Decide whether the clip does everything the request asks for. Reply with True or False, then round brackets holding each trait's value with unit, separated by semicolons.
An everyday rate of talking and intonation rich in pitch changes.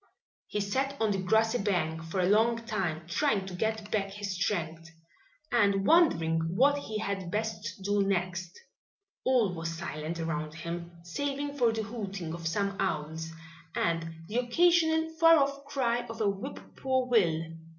True (160 wpm; 5.9 semitones)